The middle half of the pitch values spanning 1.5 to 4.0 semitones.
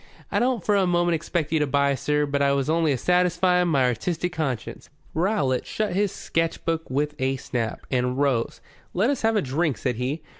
No: average, 4.9 semitones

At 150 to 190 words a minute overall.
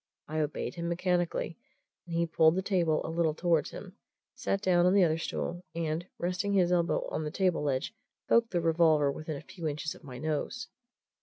No: average, 200 wpm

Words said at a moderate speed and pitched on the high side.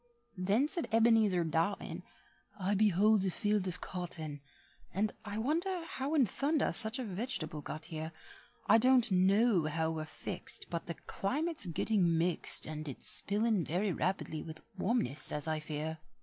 Yes: average, 155 wpm; high, 195 Hz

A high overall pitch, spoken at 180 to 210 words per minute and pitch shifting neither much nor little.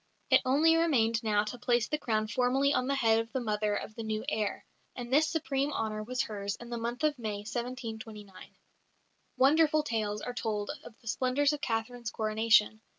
Yes: high, 235 Hz; average, 190 wpm; average, 3.5 semitones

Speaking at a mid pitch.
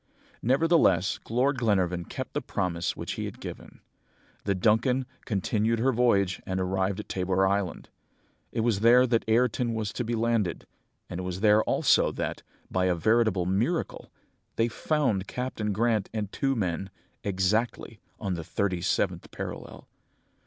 No: low, 105 Hz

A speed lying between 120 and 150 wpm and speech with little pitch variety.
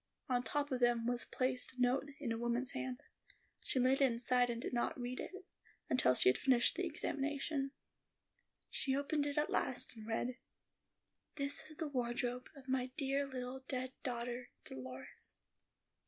No: average, 170 wpm; narrow, 2.1 semitones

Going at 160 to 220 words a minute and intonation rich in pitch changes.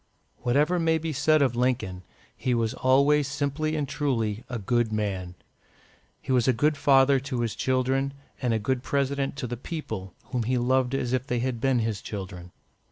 No: average, 185 wpm; average, 3.3 semitones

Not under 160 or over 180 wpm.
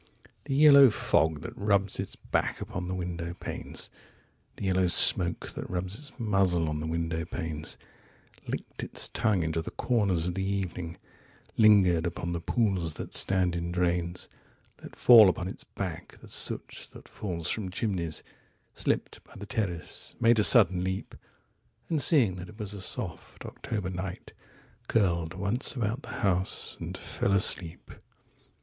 No: average, 145 wpm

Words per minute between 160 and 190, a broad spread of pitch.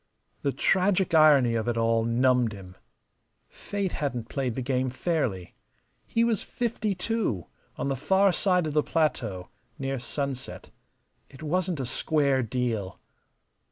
No: average, 140 wpm; wide, 6.9 semitones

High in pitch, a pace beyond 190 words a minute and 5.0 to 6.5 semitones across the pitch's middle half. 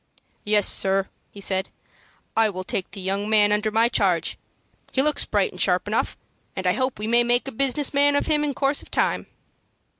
Yes: high, 220 Hz; fast, 205 wpm; wide, 5.4 semitones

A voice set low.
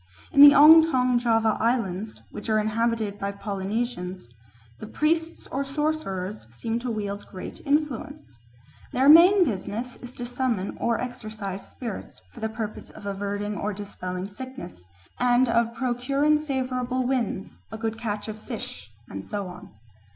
No: high, 230 Hz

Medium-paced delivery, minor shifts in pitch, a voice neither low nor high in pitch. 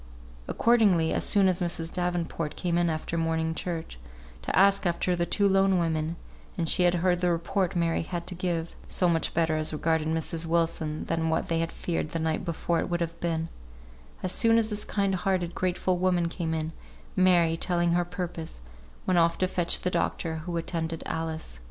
Yes: average, 195 wpm; narrow, 1.8 semitones; medium, 170 Hz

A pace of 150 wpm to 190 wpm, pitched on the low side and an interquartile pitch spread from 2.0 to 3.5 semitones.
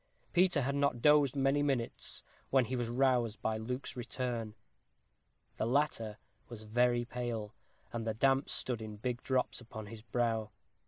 Yes: average, 155 wpm; low, 120 Hz; average, 3.0 semitones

